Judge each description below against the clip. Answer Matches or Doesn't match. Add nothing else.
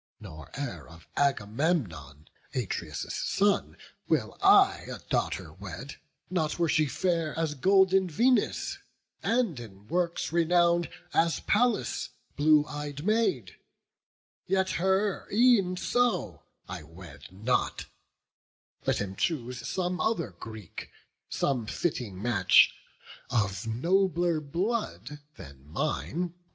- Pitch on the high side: Doesn't match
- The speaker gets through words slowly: Matches